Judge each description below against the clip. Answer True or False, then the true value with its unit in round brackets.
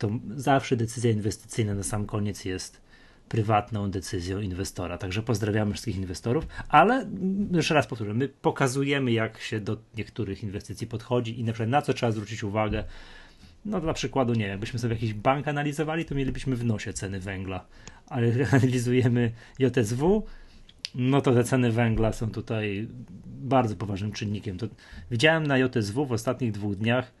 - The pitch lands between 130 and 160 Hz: False (115 Hz)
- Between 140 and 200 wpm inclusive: True (160 wpm)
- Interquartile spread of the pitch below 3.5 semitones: False (4.0 semitones)